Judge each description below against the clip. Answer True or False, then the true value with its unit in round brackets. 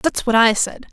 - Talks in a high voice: True (240 Hz)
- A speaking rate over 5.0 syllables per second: False (4.8 syllables/s)